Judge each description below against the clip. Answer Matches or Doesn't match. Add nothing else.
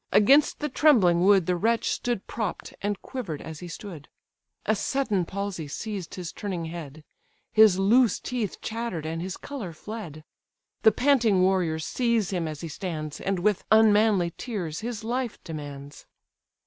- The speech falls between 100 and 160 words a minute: Matches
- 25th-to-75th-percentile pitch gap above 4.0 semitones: Matches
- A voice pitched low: Doesn't match